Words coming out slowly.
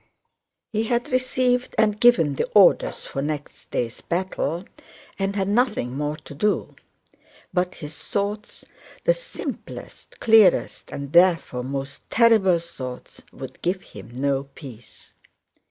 Yes: slow, 120 wpm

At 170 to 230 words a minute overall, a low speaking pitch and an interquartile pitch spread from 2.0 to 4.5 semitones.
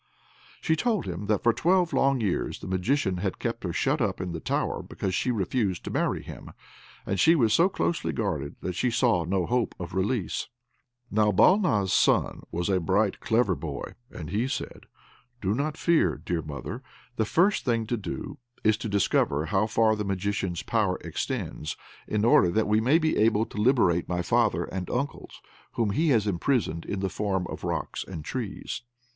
No: average, 185 wpm; low, 105 Hz; average, 4.9 semitones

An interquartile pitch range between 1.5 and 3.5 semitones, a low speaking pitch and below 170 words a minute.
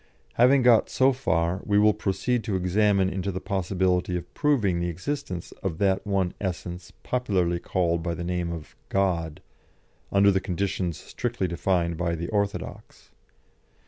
Yes: average, 2.9 semitones; very low, 95 Hz; average, 150 wpm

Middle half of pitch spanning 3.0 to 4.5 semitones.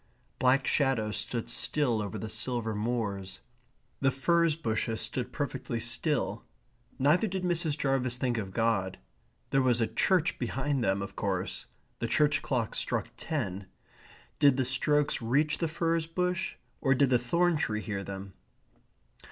No: average, 5.3 semitones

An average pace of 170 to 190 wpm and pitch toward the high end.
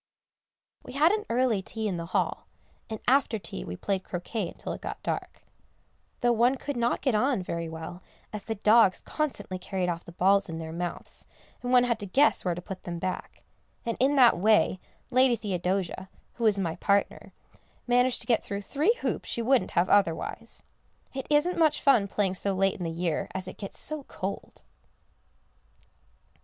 Yes: average, 185 wpm; high, 205 Hz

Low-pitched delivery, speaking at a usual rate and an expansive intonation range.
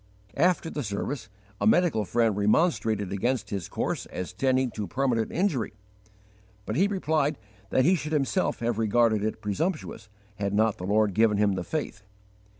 Yes: low, 115 Hz; average, 160 wpm; wide, 6.3 semitones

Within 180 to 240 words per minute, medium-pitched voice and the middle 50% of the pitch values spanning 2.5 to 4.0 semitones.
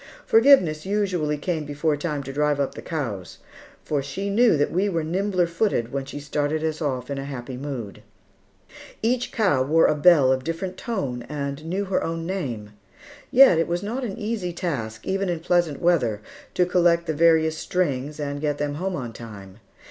No: average, 185 wpm; medium, 155 Hz; average, 4.5 semitones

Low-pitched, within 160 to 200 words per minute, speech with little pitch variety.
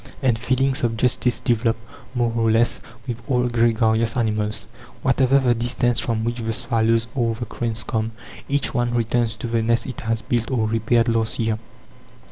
Yes: low, 115 Hz; average, 175 wpm; narrow, 1.4 semitones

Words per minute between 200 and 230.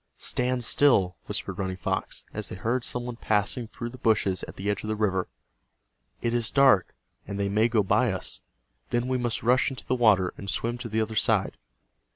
Yes: fast, 205 wpm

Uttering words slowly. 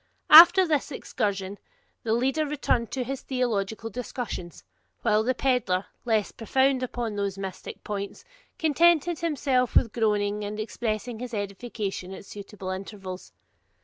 Yes: slow, 130 wpm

